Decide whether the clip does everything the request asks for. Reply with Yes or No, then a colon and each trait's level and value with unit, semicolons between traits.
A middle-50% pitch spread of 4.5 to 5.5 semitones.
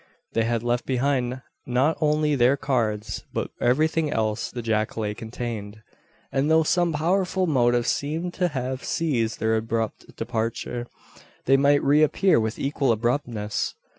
Yes: average, 4.8 semitones